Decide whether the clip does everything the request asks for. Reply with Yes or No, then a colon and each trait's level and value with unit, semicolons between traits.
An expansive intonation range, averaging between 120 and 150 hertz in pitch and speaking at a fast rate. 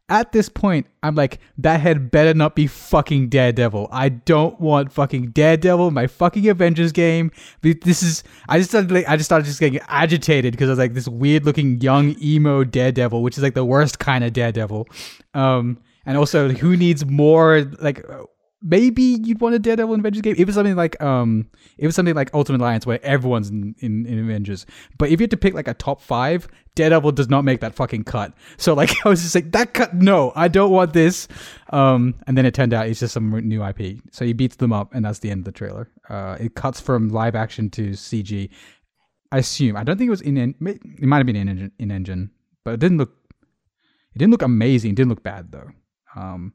Yes: wide, 5.9 semitones; medium, 140 Hz; fast, 225 wpm